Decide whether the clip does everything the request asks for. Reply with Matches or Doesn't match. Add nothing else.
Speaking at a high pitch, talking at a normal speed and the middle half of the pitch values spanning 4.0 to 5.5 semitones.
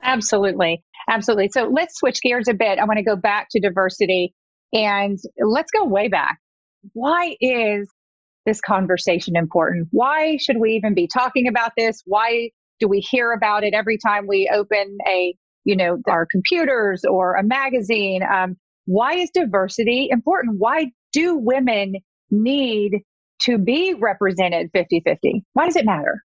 Matches